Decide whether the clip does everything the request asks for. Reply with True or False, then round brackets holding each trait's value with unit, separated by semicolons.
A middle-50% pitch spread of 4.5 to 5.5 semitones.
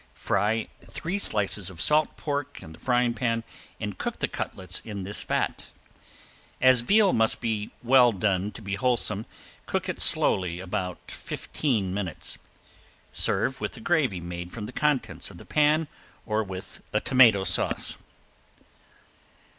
True (5.2 semitones)